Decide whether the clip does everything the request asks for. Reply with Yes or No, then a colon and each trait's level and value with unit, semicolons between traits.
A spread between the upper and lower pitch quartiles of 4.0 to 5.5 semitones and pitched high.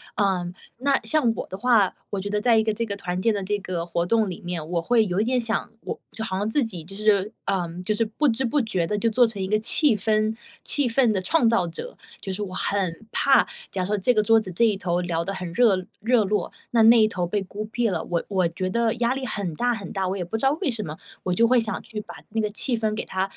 No: average, 3.6 semitones; high, 210 Hz